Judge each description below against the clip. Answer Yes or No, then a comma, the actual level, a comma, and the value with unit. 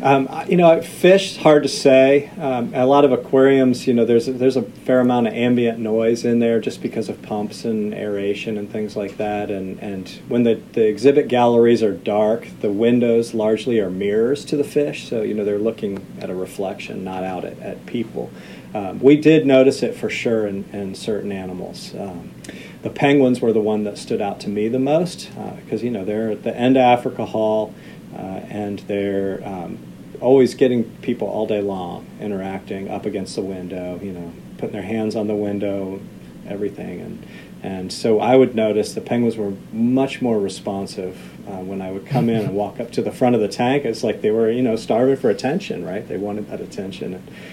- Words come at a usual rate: No, fast, 210 wpm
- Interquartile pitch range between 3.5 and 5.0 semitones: Yes, average, 3.9 semitones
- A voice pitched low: Yes, low, 115 Hz